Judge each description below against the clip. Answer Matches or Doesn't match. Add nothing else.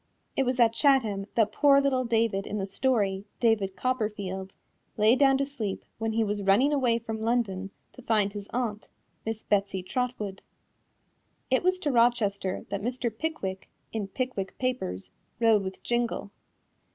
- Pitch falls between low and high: Doesn't match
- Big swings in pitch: Doesn't match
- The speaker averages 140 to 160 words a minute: Matches